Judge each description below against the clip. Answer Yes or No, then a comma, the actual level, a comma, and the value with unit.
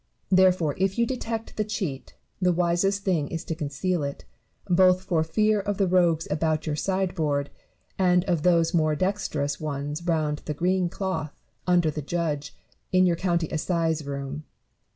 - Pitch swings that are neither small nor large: Yes, average, 3.4 semitones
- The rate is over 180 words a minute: No, average, 160 wpm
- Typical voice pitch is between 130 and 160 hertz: No, medium, 170 Hz